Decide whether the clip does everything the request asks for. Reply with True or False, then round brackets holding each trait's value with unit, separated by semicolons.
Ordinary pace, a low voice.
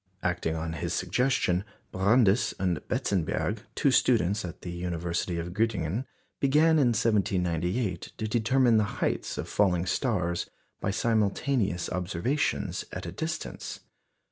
False (125 wpm; 100 Hz)